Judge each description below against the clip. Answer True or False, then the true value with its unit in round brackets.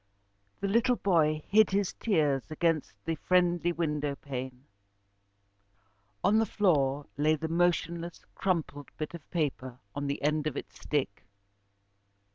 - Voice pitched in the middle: True (155 Hz)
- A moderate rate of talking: False (130 wpm)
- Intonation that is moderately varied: True (3.5 semitones)